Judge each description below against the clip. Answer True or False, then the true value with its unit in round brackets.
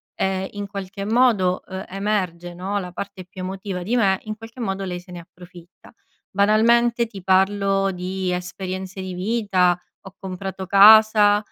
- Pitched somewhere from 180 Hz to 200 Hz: True (190 Hz)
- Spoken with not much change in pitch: True (2.0 semitones)